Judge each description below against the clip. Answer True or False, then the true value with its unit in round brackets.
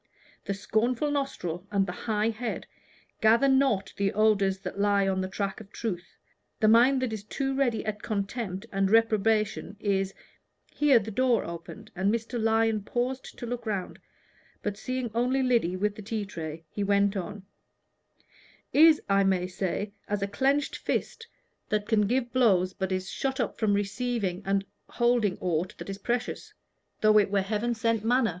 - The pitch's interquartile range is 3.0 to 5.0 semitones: True (3.4 semitones)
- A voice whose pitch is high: True (215 Hz)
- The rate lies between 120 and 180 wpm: True (175 wpm)